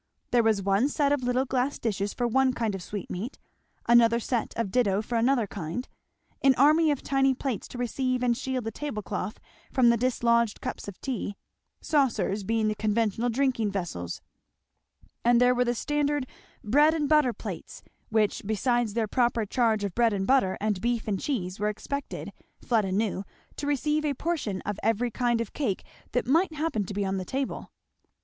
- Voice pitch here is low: No, high, 235 Hz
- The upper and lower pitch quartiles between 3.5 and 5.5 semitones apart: Yes, average, 4.1 semitones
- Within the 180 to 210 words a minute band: Yes, average, 185 wpm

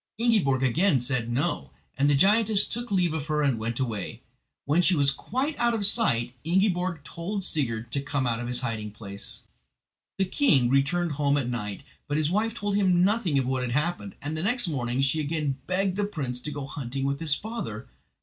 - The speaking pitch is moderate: Yes, medium, 145 Hz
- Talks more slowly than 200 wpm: No, fast, 205 wpm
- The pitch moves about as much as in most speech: No, wide, 6.9 semitones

